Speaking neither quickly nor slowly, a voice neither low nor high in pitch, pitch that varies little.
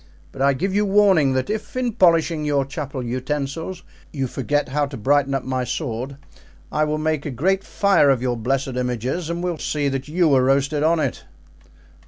No: average, 195 wpm; medium, 145 Hz; average, 3.8 semitones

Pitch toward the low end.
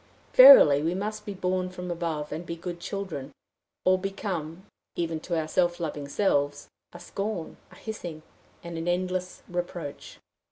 No: medium, 175 Hz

